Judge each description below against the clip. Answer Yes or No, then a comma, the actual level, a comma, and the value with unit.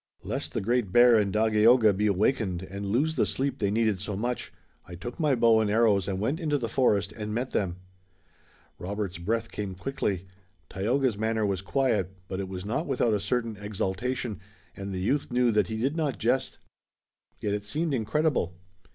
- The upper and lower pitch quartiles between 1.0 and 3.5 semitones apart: No, average, 4.0 semitones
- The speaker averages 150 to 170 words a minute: No, average, 185 wpm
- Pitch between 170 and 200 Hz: No, low, 110 Hz